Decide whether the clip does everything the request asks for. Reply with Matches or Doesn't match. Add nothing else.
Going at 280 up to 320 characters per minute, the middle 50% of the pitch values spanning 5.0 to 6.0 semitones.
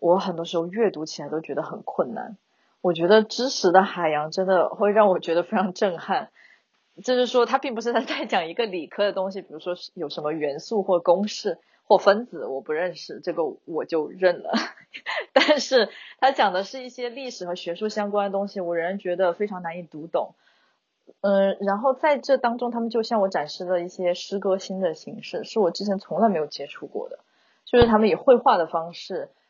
Matches